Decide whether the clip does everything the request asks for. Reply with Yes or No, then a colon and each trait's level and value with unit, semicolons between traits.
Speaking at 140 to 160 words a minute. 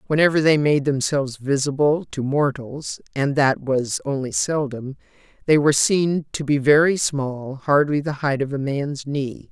Yes: average, 150 wpm